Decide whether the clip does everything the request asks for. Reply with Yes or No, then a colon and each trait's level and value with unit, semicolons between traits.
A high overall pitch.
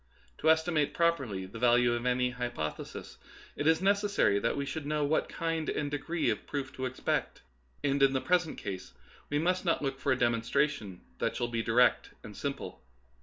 No: medium, 140 Hz